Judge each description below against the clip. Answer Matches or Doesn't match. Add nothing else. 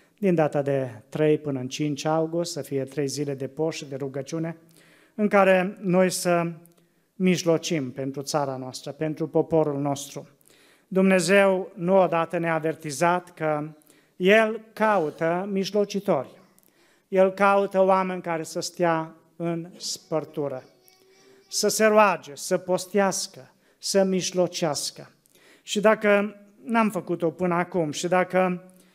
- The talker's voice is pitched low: Doesn't match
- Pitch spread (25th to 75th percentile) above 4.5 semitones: Doesn't match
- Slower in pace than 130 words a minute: Matches